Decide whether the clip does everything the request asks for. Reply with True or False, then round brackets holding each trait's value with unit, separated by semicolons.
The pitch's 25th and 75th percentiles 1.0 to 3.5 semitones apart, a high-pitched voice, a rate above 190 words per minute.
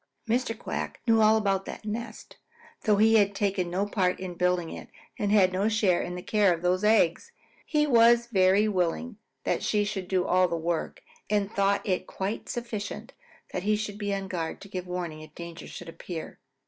True (3.0 semitones; 195 Hz; 200 wpm)